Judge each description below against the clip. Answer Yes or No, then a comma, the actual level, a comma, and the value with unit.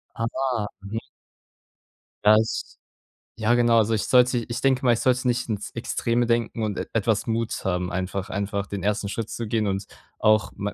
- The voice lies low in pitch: Yes, low, 110 Hz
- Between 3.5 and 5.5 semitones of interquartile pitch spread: No, average, 2.8 semitones